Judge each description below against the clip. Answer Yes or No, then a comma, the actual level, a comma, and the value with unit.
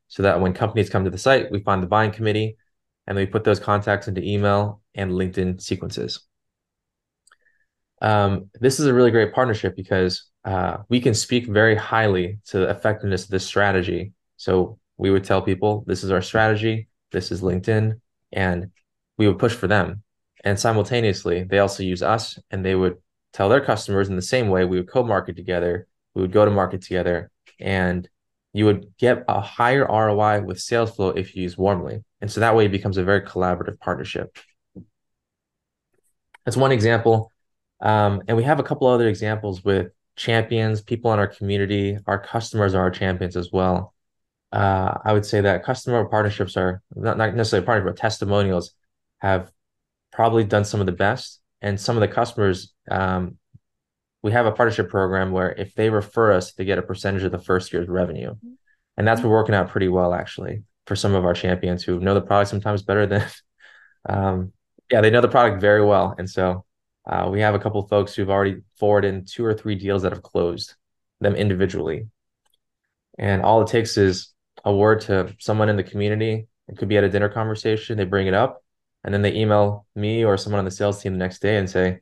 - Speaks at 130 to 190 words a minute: No, average, 200 wpm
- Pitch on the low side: Yes, low, 100 Hz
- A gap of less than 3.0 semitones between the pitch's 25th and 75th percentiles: Yes, narrow, 2.6 semitones